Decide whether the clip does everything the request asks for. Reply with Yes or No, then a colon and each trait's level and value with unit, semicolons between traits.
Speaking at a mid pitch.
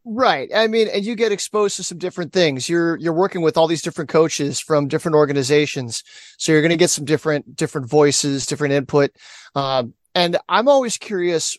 Yes: medium, 160 Hz